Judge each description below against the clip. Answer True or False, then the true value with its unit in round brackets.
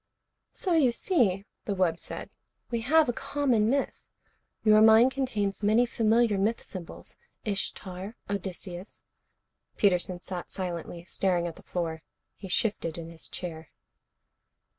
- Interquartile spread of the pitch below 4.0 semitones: False (4.6 semitones)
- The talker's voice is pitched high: True (200 Hz)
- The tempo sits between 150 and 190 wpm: False (135 wpm)